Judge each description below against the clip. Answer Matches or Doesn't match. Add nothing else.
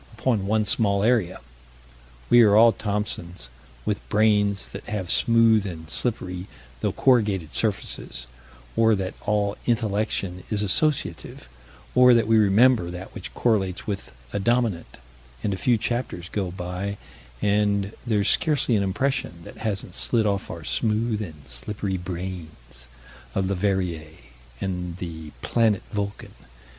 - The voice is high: Doesn't match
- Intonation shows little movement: Doesn't match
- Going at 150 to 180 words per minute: Doesn't match